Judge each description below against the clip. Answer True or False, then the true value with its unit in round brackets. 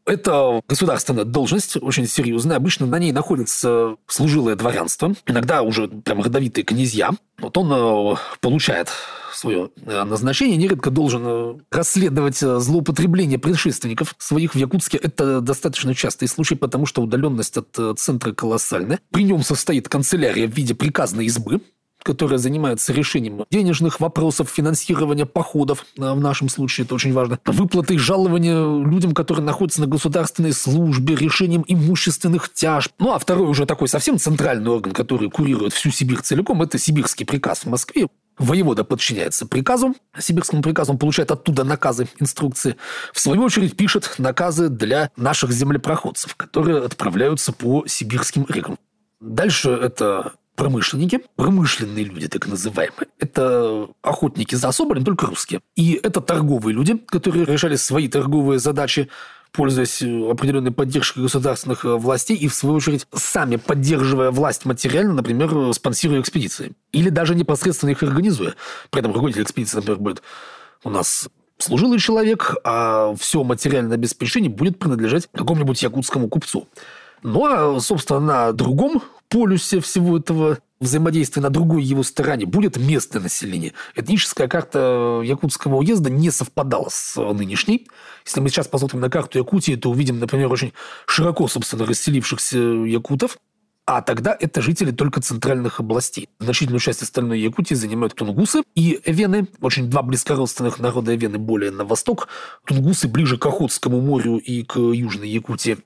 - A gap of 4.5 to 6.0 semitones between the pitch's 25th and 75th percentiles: True (5.0 semitones)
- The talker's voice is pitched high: False (145 Hz)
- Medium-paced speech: True (140 wpm)